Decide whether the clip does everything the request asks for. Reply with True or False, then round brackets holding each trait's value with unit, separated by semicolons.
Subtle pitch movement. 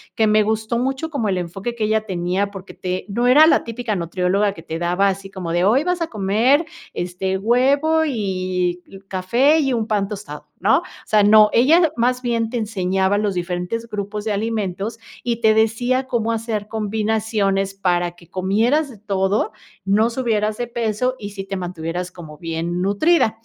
False (3.7 semitones)